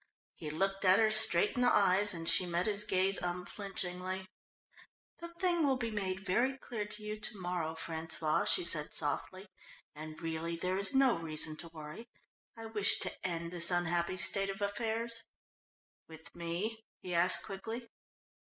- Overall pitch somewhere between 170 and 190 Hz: Yes, medium, 185 Hz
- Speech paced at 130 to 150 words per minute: No, average, 165 wpm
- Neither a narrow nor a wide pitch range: Yes, average, 4.1 semitones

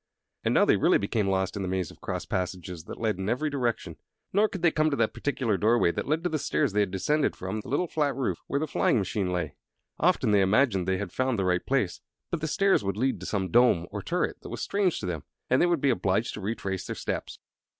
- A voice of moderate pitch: No, low, 110 Hz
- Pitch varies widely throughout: Yes, wide, 6.9 semitones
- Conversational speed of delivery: No, fast, 255 wpm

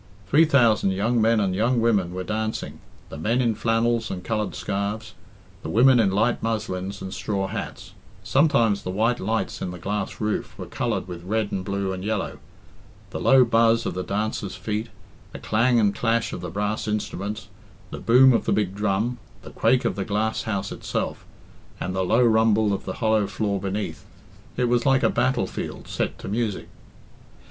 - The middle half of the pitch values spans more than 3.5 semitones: No, average, 2.8 semitones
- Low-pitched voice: Yes, low, 110 Hz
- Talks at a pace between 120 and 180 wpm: No, average, 190 wpm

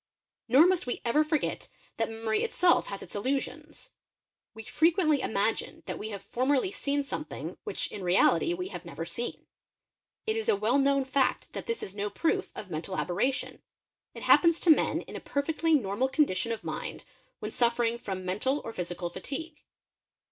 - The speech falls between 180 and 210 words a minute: No, average, 170 wpm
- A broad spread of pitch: Yes, wide, 7.1 semitones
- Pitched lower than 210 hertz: No, very high, 250 Hz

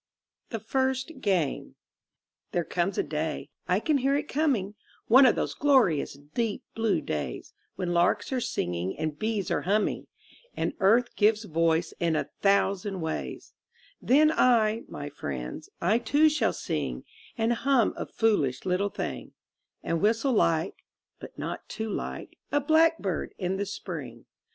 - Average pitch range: No, wide, 6.5 semitones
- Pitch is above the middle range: Yes, high, 205 Hz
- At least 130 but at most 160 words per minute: Yes, average, 150 wpm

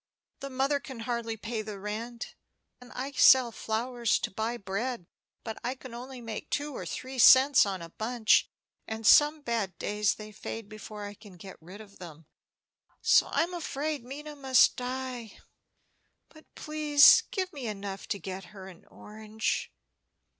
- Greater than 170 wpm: No, average, 160 wpm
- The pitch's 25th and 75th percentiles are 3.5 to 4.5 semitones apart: Yes, average, 4.1 semitones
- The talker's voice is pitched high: Yes, high, 230 Hz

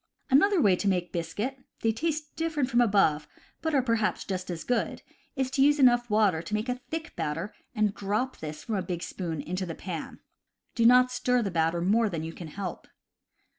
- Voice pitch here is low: No, high, 215 Hz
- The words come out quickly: Yes, fast, 210 wpm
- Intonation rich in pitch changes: Yes, wide, 6.2 semitones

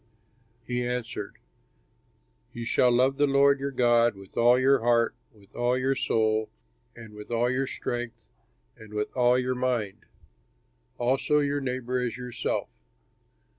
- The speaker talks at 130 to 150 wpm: Yes, average, 140 wpm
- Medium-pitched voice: No, low, 125 Hz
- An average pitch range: No, narrow, 1.7 semitones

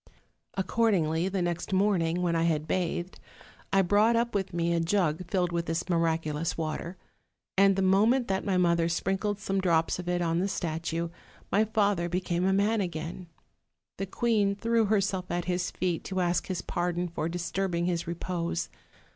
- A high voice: No, medium, 180 Hz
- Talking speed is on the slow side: No, average, 175 wpm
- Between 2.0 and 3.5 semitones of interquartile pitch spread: Yes, narrow, 2.5 semitones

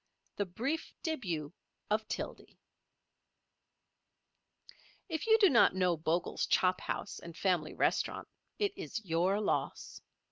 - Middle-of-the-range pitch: No, high, 195 Hz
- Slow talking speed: Yes, slow, 115 wpm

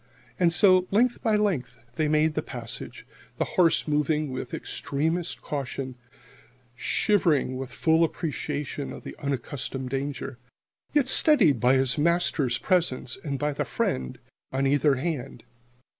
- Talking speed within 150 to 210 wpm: No, slow, 135 wpm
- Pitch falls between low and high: Yes, medium, 150 Hz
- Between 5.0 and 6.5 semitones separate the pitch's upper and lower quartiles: No, average, 4.2 semitones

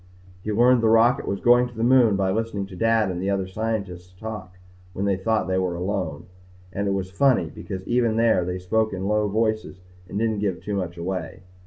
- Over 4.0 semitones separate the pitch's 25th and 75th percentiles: No, average, 3.3 semitones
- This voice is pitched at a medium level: No, low, 100 Hz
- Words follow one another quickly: Yes, fast, 215 wpm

